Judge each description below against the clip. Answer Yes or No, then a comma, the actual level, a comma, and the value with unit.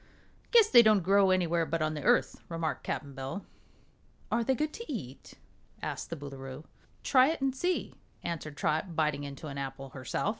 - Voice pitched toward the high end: No, medium, 165 Hz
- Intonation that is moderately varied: No, wide, 8.4 semitones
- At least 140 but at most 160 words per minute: No, average, 180 wpm